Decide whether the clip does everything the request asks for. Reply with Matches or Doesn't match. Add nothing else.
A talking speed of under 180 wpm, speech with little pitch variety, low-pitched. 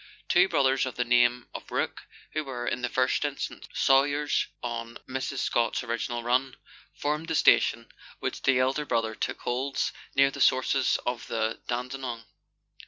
Matches